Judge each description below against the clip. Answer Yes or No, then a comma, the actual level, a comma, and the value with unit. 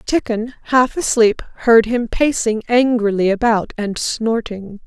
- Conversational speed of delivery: No, slow, 125 wpm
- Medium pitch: No, high, 225 Hz